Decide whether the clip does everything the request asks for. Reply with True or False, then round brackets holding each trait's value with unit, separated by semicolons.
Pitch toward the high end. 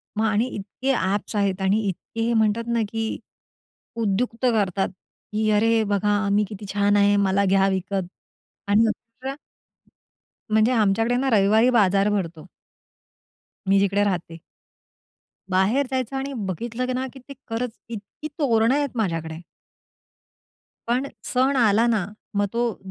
True (215 Hz)